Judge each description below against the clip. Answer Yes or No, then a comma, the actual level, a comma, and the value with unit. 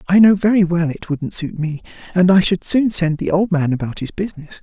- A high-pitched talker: No, medium, 175 Hz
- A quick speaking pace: Yes, fast, 245 wpm